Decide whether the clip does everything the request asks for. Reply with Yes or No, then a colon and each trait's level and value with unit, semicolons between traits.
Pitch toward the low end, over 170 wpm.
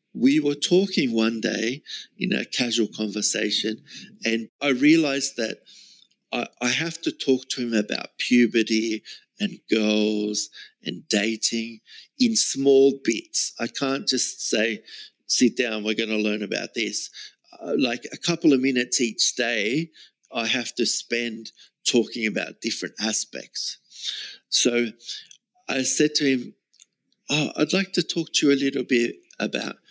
No: low, 125 Hz; average, 145 wpm